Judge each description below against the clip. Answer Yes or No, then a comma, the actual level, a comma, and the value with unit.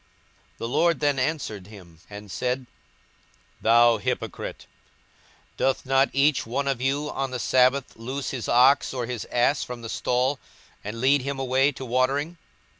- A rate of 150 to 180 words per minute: Yes, average, 160 wpm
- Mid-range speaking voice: No, low, 130 Hz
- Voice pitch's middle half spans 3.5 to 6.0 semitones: No, average, 2.7 semitones